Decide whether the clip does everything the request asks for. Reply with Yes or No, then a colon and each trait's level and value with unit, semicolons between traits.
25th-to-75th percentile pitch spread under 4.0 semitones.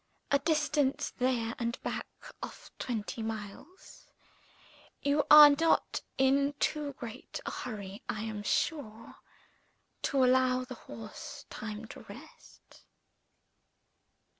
No: average, 4.5 semitones